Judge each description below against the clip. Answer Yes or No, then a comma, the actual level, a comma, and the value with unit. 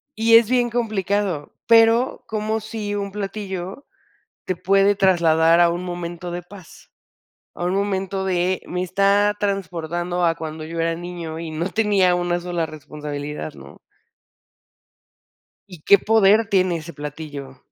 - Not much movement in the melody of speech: No, average, 3.4 semitones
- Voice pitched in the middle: Yes, medium, 180 Hz